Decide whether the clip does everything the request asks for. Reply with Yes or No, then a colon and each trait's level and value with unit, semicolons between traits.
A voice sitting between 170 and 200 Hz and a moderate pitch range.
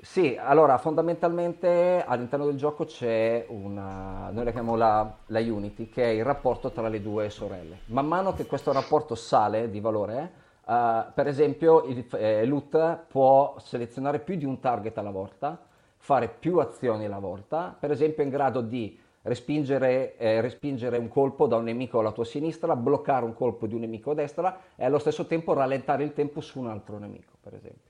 No: low, 130 Hz; average, 4.7 semitones